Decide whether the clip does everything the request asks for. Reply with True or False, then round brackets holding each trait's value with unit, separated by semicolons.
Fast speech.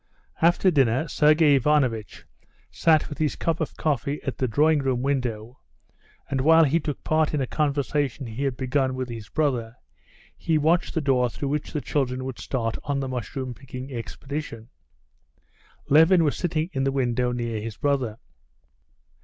False (165 wpm)